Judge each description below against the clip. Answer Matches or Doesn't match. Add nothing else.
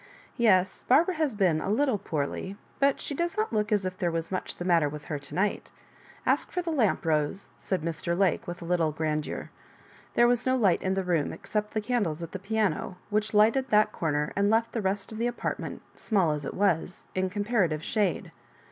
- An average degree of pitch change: Matches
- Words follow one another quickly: Matches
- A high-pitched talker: Matches